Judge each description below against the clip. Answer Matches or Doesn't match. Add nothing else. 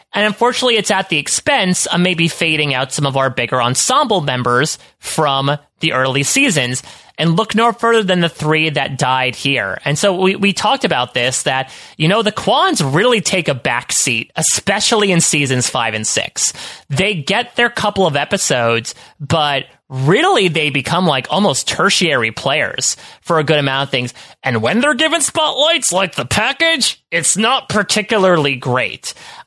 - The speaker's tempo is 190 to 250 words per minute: Doesn't match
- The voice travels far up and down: Matches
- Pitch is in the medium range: Matches